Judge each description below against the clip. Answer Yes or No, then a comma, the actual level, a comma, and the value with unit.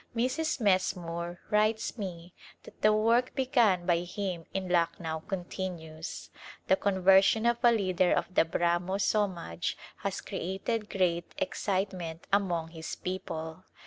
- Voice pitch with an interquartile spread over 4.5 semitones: No, average, 3.6 semitones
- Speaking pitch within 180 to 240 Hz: Yes, medium, 185 Hz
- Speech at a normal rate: No, slow, 130 wpm